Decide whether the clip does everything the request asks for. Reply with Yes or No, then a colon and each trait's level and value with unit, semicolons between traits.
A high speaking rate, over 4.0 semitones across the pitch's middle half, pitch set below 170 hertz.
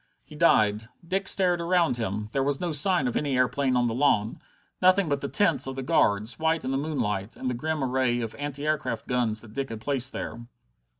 Yes: fast, 220 wpm; average, 4.5 semitones; low, 135 Hz